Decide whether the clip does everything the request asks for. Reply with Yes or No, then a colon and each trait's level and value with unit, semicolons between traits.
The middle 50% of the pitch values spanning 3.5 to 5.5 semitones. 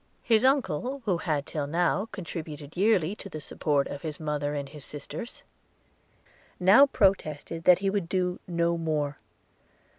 Yes: average, 4.6 semitones